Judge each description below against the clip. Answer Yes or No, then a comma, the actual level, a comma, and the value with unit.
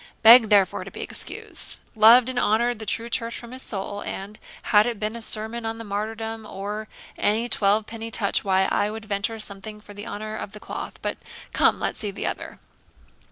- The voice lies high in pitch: Yes, high, 215 Hz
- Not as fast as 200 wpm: No, fast, 205 wpm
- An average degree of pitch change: No, narrow, 1.8 semitones